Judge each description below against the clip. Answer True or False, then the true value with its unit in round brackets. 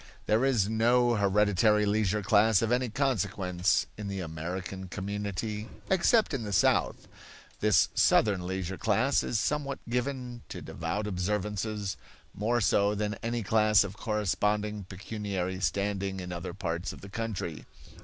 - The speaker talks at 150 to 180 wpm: False (140 wpm)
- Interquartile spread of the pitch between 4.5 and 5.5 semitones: False (2.7 semitones)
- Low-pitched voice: True (105 Hz)